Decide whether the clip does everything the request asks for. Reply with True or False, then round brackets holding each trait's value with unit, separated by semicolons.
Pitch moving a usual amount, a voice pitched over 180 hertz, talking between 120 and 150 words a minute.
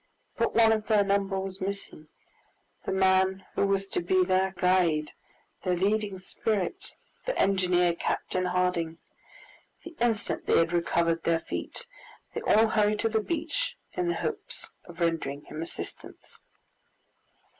True (3.3 semitones; 190 Hz; 145 wpm)